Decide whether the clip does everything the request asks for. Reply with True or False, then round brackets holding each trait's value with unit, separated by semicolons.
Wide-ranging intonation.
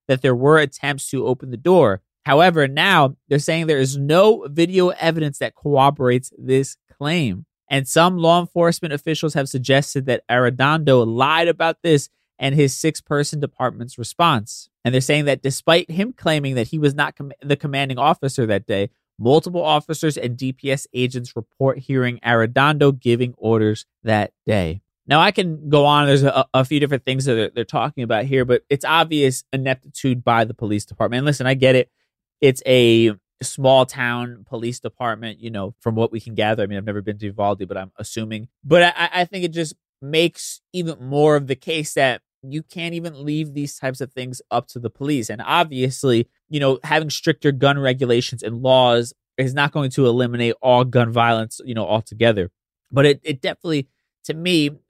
False (3.9 semitones)